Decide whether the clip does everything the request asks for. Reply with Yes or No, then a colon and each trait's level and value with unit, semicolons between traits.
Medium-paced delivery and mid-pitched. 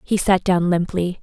Yes: average, 195 wpm; medium, 180 Hz